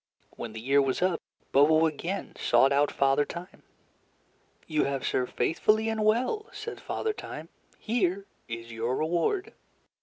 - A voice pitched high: No, medium, 160 Hz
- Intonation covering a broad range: Yes, wide, 7.8 semitones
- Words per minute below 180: Yes, average, 145 wpm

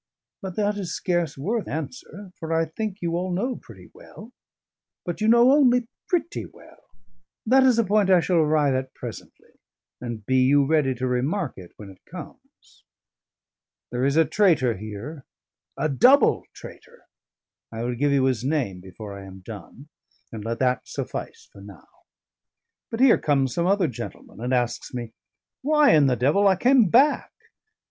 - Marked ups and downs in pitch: Yes, wide, 8.7 semitones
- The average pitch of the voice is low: No, medium, 155 Hz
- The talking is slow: No, average, 170 wpm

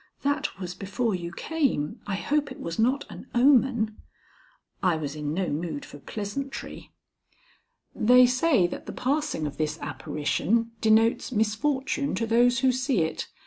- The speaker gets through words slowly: No, average, 150 wpm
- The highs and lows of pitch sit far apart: Yes, wide, 6.9 semitones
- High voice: Yes, high, 225 Hz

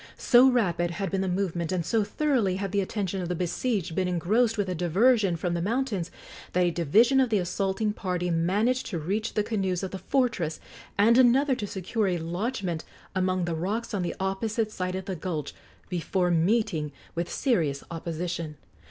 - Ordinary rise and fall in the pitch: Yes, average, 4.1 semitones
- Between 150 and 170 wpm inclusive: No, average, 185 wpm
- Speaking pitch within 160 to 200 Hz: Yes, high, 190 Hz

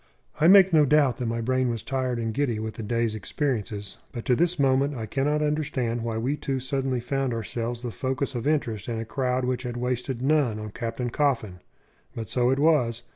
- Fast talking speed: Yes, fast, 210 wpm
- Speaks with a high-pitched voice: No, low, 125 Hz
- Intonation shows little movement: No, average, 3.1 semitones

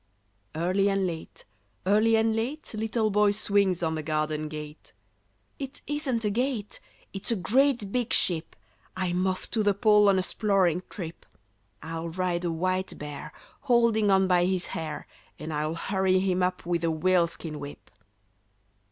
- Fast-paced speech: No, average, 160 wpm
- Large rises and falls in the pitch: No, average, 4.3 semitones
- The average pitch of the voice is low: No, medium, 185 Hz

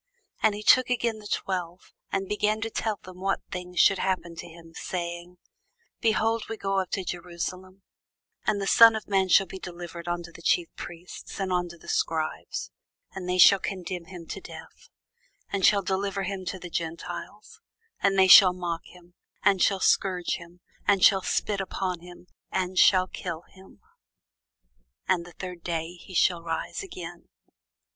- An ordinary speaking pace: Yes, average, 170 wpm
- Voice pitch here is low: No, medium, 185 Hz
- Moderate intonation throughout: No, narrow, 2.1 semitones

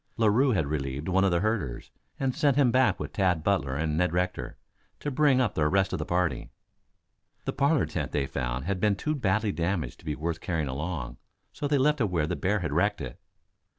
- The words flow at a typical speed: No, fast, 220 wpm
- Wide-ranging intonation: Yes, wide, 6.6 semitones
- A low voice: Yes, very low, 95 Hz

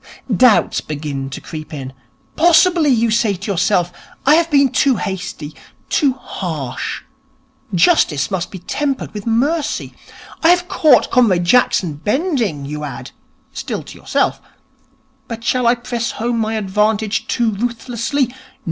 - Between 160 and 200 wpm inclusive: No, average, 140 wpm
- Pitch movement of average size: No, wide, 6.8 semitones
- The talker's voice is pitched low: No, high, 225 Hz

